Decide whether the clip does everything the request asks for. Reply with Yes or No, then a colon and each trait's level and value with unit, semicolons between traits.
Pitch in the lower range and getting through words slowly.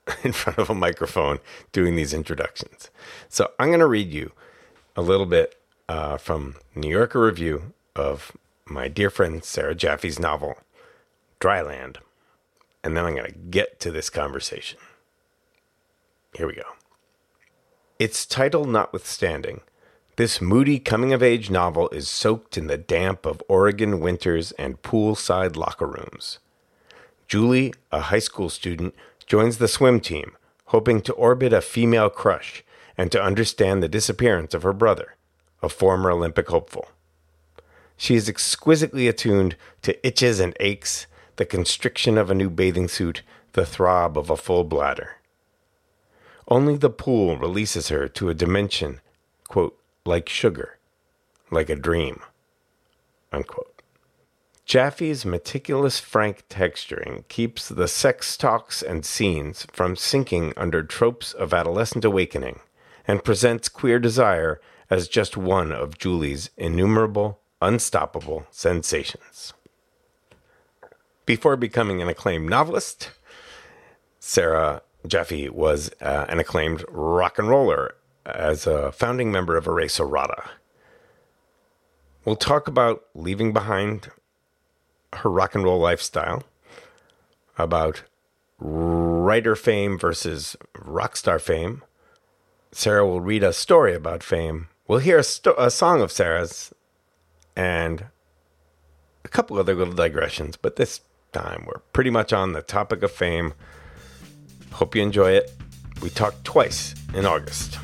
Yes: low, 110 Hz; slow, 130 wpm